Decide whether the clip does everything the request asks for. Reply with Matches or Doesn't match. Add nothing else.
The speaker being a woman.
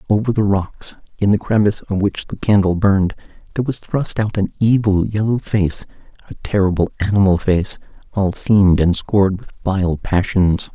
Doesn't match